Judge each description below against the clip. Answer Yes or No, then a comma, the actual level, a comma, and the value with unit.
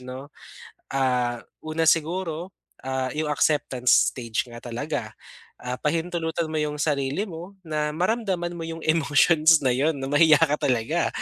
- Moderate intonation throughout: Yes, average, 3.7 semitones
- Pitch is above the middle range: No, medium, 150 Hz